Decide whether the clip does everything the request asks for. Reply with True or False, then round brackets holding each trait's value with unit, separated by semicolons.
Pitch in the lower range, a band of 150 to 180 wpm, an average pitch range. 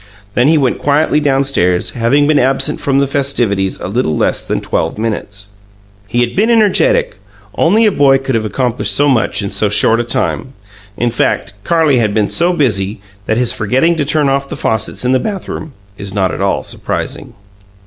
False (130 Hz; 190 wpm; 5.0 semitones)